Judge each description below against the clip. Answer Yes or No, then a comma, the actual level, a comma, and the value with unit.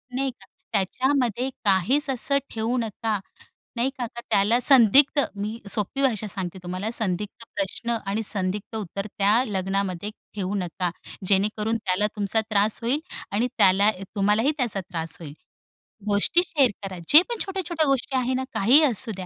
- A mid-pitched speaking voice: No, high, 215 Hz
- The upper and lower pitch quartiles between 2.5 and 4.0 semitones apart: No, average, 4.6 semitones